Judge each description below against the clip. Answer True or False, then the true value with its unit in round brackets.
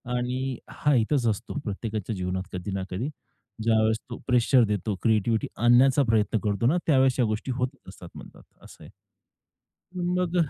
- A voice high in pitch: False (115 Hz)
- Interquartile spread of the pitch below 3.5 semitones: False (3.9 semitones)